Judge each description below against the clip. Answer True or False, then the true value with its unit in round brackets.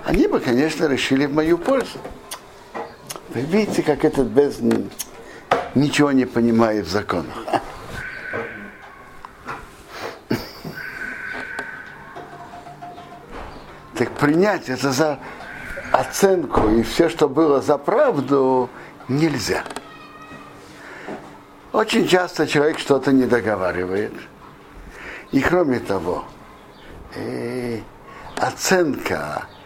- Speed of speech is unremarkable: False (80 wpm)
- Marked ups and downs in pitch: True (6.0 semitones)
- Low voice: False (145 Hz)